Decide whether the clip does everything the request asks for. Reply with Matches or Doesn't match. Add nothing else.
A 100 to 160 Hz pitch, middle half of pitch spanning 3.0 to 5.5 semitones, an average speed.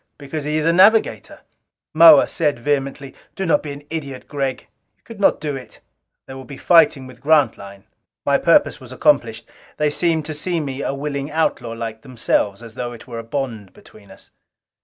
Matches